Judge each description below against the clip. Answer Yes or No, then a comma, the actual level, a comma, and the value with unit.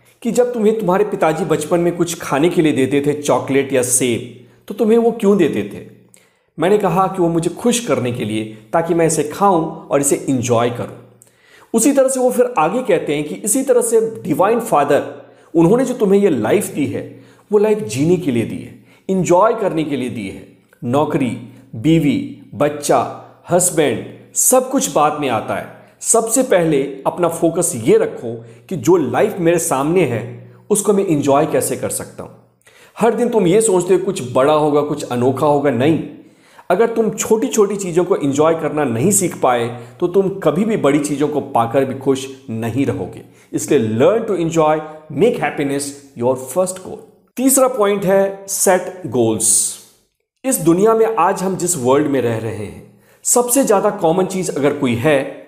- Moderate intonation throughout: No, wide, 6.8 semitones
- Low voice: No, medium, 165 Hz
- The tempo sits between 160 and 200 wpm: Yes, average, 185 wpm